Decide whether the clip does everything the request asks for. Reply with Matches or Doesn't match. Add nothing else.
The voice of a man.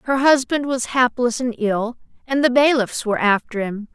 Doesn't match